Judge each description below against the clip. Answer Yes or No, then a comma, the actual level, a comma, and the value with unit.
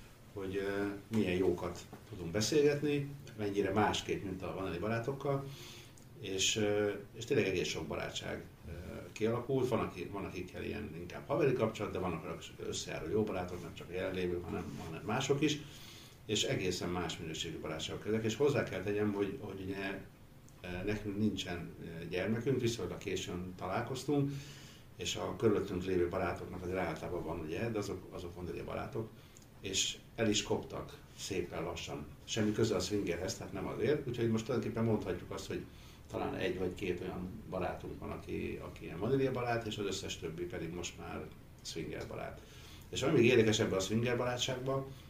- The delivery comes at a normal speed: No, fast, 160 wpm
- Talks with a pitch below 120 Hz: Yes, low, 105 Hz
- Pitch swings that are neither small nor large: Yes, average, 4.3 semitones